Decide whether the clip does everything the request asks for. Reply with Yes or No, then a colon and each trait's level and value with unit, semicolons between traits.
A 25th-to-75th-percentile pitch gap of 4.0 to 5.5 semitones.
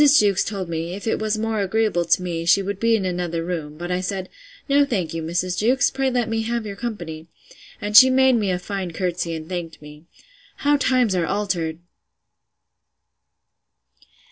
Yes: average, 4.6 semitones